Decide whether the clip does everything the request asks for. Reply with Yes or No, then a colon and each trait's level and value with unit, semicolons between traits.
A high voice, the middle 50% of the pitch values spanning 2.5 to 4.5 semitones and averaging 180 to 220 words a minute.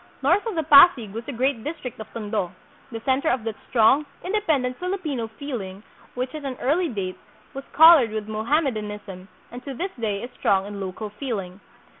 No: high, 245 Hz; wide, 5.4 semitones; average, 185 wpm